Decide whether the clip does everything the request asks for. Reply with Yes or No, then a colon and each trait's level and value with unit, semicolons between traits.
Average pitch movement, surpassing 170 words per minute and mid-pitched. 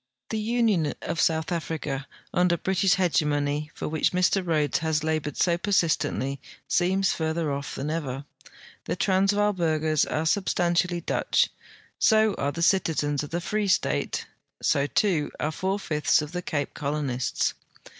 No: average, 3.8 semitones; average, 145 wpm; medium, 160 Hz